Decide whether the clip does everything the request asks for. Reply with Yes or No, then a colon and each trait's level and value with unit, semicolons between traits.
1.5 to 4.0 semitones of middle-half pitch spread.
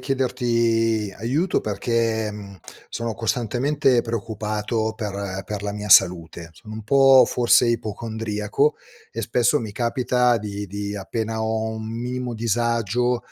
Yes: narrow, 2.5 semitones